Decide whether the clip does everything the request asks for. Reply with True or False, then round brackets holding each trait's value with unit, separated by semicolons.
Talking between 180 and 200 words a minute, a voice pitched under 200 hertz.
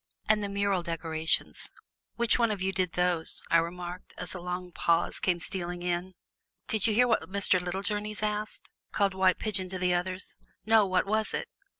True (185 wpm; 185 Hz)